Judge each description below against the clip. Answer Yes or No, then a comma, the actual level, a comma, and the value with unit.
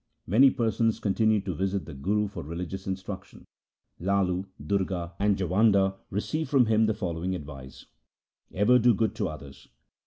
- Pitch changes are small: No, average, 3.2 semitones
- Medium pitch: No, very low, 95 Hz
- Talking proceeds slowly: No, average, 155 wpm